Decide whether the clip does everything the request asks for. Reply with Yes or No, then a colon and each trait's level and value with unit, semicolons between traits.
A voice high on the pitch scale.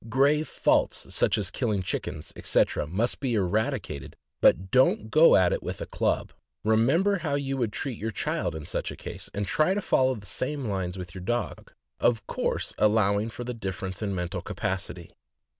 No: low, 110 Hz